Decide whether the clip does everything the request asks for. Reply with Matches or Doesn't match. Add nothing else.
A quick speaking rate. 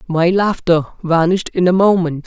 Doesn't match